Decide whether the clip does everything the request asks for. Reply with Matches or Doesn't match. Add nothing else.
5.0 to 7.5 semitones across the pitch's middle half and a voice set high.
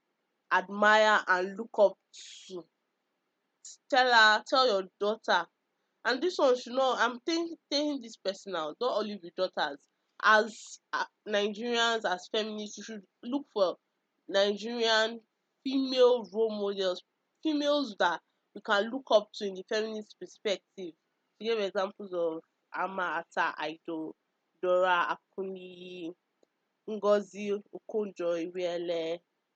Doesn't match